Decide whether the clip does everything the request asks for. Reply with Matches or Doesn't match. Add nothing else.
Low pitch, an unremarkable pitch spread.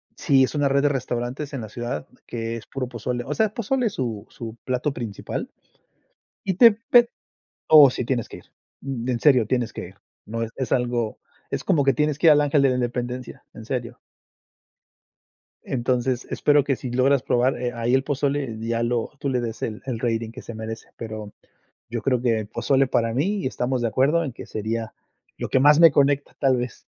Matches